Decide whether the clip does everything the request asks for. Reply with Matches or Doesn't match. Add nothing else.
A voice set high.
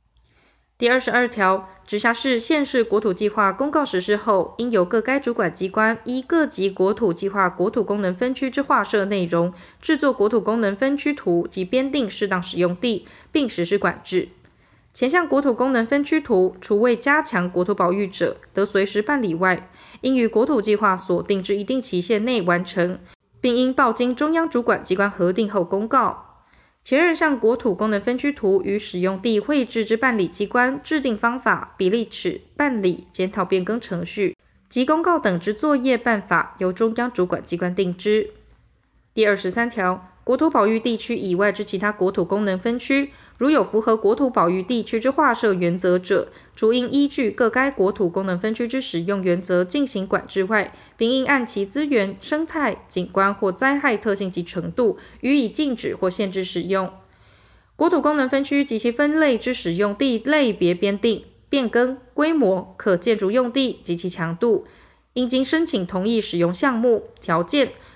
Matches